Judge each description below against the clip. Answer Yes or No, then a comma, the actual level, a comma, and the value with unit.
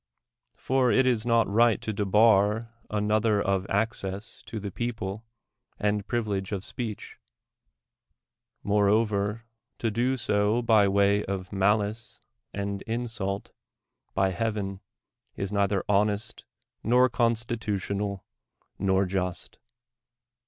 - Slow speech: Yes, slow, 110 wpm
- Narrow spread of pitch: Yes, narrow, 2.3 semitones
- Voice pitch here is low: Yes, low, 105 Hz